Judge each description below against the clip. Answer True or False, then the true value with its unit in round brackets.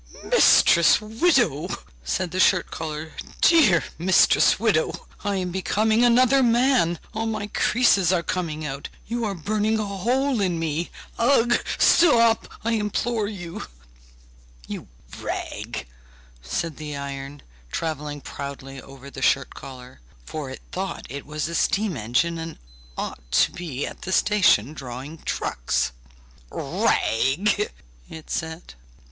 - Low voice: False (175 Hz)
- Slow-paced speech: True (130 wpm)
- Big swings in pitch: True (6.8 semitones)